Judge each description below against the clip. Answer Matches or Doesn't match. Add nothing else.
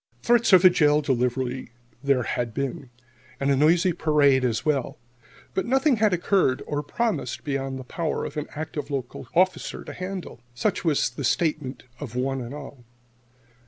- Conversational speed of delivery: Matches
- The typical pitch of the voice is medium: Matches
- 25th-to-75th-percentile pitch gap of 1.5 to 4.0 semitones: Doesn't match